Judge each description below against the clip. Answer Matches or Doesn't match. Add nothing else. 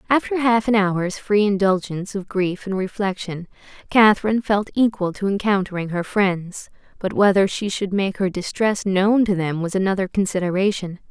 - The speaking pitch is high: Matches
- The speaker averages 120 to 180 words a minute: Matches